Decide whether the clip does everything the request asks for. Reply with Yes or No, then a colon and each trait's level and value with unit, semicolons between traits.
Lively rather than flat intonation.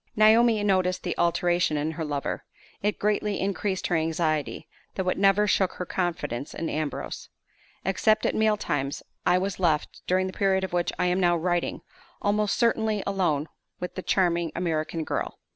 No: average, 3.3 semitones